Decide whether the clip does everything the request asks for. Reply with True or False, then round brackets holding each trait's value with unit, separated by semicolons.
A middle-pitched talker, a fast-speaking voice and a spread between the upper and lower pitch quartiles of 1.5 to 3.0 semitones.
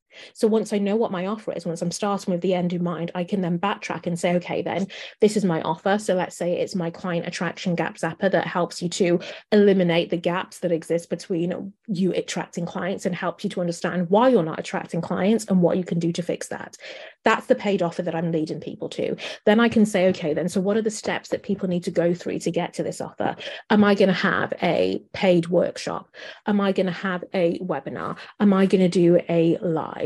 True (180 Hz; 240 wpm; 2.5 semitones)